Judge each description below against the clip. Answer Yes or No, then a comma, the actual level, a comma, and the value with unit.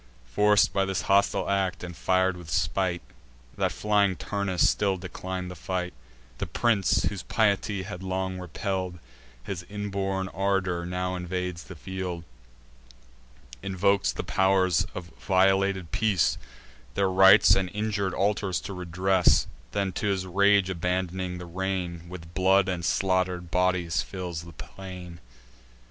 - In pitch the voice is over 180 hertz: No, very low, 95 Hz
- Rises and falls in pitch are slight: Yes, narrow, 1.4 semitones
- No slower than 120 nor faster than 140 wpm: Yes, slow, 135 wpm